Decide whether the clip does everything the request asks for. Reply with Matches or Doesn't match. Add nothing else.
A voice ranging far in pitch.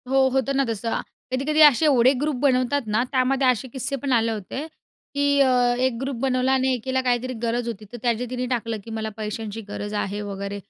Doesn't match